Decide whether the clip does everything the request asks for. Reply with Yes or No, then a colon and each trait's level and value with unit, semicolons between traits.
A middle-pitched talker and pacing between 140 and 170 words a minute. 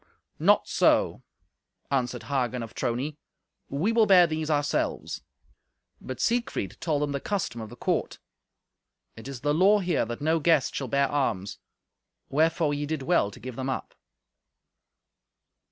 Yes: medium, 145 Hz; average, 150 wpm